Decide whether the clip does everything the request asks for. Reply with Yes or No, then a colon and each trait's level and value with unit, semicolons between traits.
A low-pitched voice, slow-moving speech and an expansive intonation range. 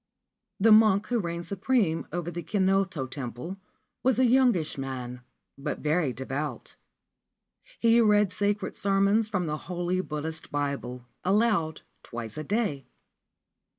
No: medium, 175 Hz; slow, 125 wpm; wide, 6.1 semitones